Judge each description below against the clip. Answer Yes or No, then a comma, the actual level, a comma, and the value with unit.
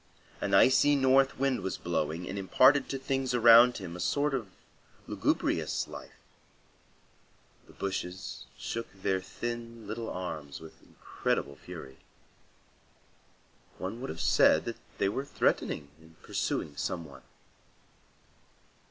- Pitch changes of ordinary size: No, wide, 7.0 semitones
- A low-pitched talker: Yes, low, 100 Hz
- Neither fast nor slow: No, slow, 125 wpm